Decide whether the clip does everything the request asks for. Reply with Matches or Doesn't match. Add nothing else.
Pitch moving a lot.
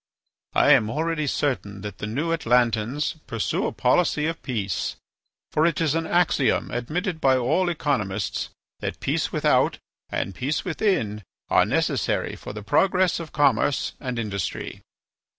Matches